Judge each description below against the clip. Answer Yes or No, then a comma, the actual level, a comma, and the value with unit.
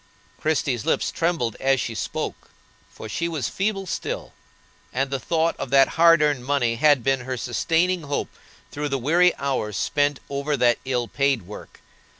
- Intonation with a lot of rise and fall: No, average, 4.2 semitones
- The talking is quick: No, average, 165 wpm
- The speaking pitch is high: No, medium, 140 Hz